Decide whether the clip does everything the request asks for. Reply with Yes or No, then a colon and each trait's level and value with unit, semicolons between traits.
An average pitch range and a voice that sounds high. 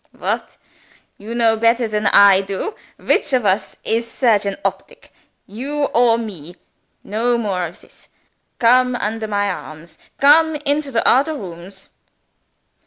Yes: average, 4.1 semitones; high, 225 Hz